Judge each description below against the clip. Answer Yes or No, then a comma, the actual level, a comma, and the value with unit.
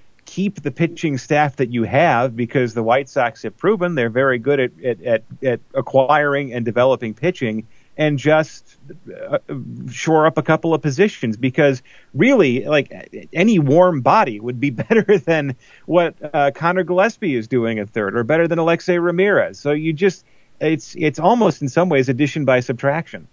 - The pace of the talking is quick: No, average, 170 wpm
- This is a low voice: No, medium, 150 Hz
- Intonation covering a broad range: No, average, 4.5 semitones